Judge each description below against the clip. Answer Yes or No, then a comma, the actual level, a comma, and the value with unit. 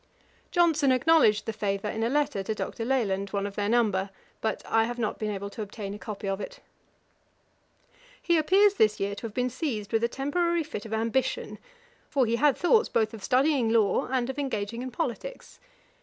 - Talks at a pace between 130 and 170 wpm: No, average, 200 wpm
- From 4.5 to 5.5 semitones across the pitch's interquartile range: Yes, average, 5.1 semitones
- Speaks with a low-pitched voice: No, high, 230 Hz